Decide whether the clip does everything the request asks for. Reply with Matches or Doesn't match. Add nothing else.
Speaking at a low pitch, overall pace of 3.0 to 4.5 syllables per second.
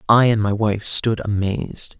Matches